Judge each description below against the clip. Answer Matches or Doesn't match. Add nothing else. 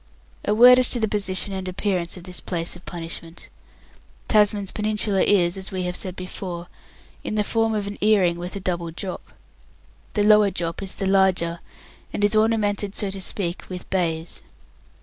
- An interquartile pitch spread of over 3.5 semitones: Doesn't match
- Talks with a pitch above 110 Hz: Matches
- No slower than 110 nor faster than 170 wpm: Doesn't match